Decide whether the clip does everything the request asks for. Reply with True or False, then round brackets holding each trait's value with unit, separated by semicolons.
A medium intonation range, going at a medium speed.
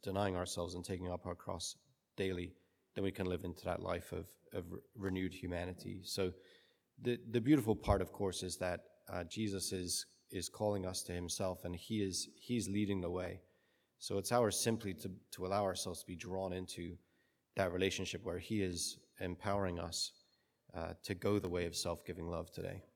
False (2.1 semitones; 190 wpm)